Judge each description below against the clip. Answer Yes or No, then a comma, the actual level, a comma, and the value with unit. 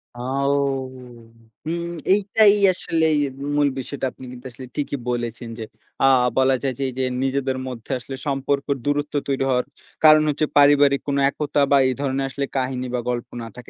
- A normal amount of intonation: No, narrow, 2.1 semitones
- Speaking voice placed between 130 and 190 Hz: Yes, medium, 140 Hz